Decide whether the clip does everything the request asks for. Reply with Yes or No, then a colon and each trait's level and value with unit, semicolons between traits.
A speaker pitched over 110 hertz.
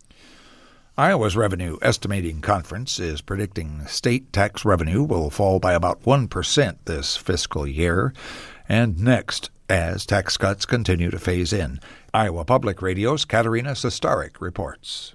No: low, 100 Hz